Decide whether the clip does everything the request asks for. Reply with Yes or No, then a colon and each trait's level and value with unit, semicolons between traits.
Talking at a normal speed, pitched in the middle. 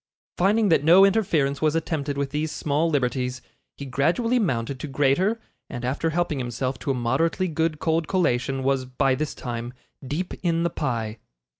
Yes: average, 170 wpm; medium, 145 Hz